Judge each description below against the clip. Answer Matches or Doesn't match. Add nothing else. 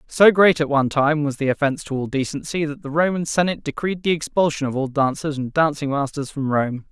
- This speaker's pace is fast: Matches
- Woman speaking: Doesn't match